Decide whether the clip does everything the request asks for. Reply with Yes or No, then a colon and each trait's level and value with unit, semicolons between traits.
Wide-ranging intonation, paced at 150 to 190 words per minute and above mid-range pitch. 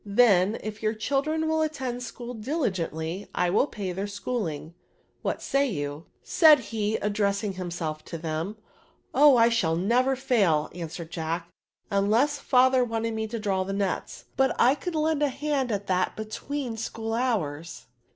Yes: wide, 5.9 semitones; average, 165 wpm; high, 215 Hz